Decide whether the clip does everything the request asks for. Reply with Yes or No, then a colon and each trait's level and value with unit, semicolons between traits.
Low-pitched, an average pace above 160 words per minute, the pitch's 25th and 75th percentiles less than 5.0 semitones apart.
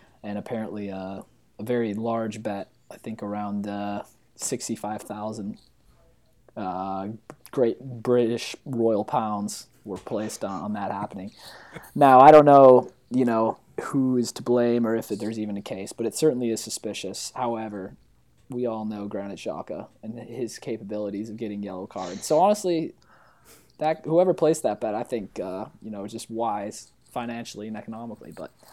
No: low, 110 Hz; average, 150 wpm; average, 2.9 semitones